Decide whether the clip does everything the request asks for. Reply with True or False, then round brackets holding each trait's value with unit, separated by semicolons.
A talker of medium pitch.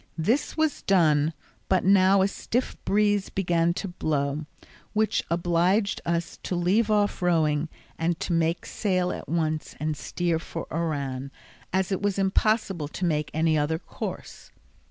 True (175 Hz)